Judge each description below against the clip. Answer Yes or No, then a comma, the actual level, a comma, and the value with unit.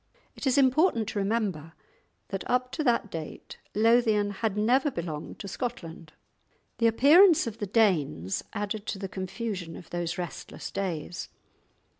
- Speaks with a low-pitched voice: No, high, 205 Hz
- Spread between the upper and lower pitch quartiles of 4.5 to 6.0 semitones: Yes, average, 5.1 semitones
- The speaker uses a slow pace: No, average, 145 wpm